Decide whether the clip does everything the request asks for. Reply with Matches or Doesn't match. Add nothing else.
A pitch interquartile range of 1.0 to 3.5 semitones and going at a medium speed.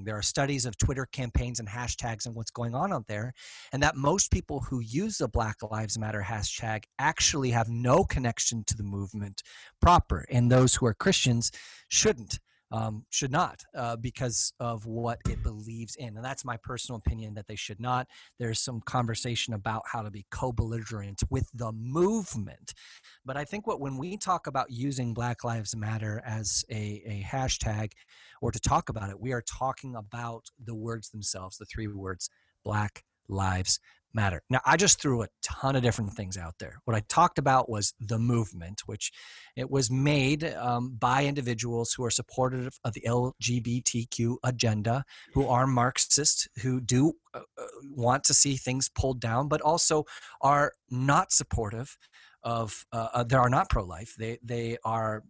Matches